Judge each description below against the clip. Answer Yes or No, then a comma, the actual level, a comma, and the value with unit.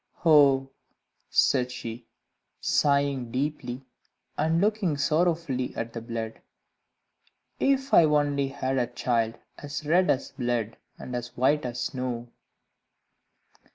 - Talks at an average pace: No, slow, 115 wpm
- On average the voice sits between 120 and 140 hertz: Yes, low, 135 Hz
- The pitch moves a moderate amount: Yes, average, 3.6 semitones